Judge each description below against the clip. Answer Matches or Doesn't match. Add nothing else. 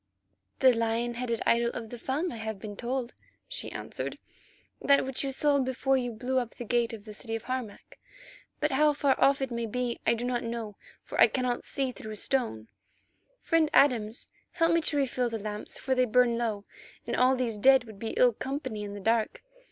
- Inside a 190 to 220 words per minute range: Matches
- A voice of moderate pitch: Doesn't match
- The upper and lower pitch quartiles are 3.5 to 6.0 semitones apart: Doesn't match